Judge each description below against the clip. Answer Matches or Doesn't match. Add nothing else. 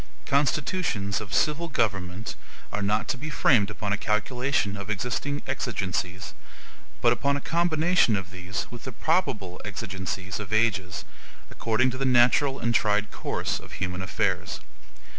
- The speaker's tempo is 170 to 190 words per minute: Doesn't match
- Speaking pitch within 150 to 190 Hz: Doesn't match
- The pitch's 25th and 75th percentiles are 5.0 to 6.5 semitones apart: Matches